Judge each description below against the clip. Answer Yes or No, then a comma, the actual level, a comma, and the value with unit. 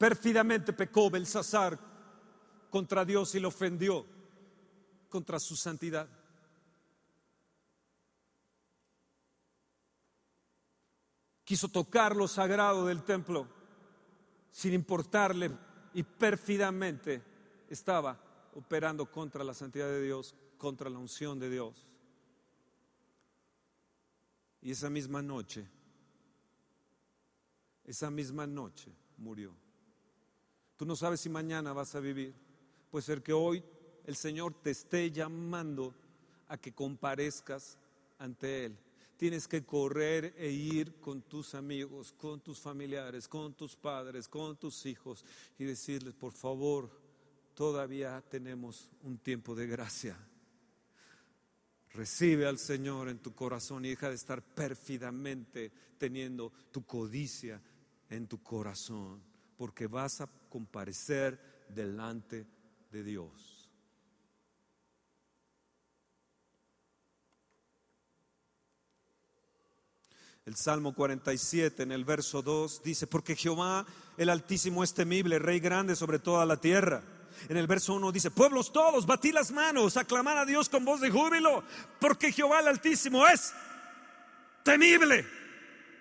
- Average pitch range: No, wide, 6.9 semitones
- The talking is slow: Yes, slow, 110 wpm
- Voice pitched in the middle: Yes, medium, 145 Hz